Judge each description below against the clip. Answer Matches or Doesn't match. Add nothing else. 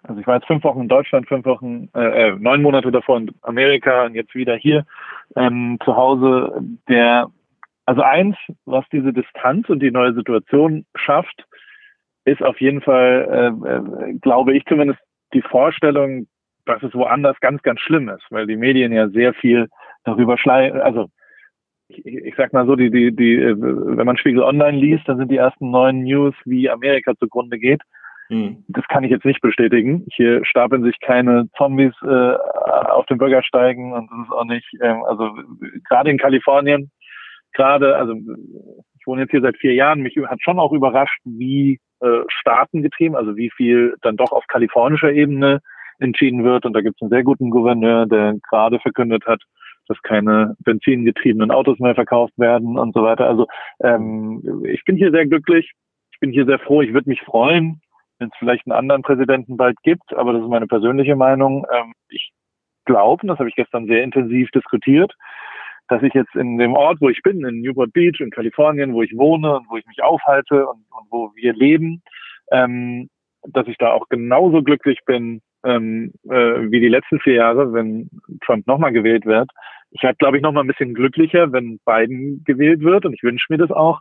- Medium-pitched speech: Doesn't match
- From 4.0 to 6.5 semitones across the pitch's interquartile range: Doesn't match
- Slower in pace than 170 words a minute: Doesn't match